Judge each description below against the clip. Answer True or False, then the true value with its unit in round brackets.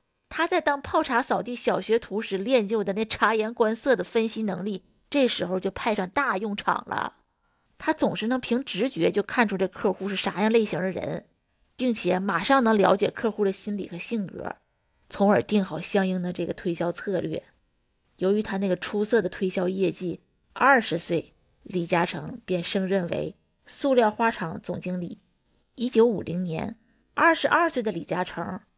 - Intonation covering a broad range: False (4.1 semitones)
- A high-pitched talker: True (205 Hz)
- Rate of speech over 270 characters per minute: False (260 characters per minute)